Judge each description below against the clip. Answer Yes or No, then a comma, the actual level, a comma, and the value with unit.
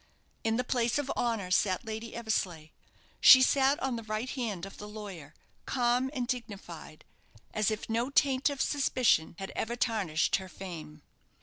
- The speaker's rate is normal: Yes, average, 165 wpm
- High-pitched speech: Yes, high, 225 Hz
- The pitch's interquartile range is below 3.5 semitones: No, average, 4.8 semitones